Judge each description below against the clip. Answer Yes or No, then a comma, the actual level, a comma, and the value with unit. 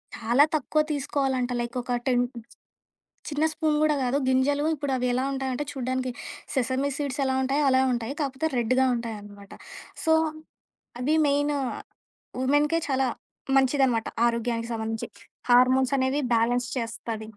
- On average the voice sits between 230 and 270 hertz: Yes, very high, 260 Hz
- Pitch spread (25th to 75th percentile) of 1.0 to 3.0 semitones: Yes, average, 2.7 semitones